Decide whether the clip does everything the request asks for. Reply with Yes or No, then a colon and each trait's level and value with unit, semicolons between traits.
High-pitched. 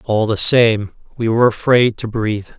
No: low, 110 Hz